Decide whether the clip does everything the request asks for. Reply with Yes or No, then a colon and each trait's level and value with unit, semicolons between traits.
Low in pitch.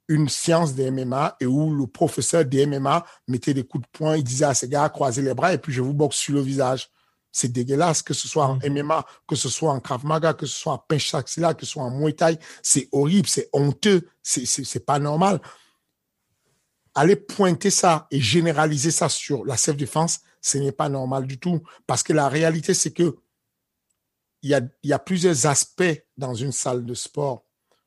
No: medium, 145 Hz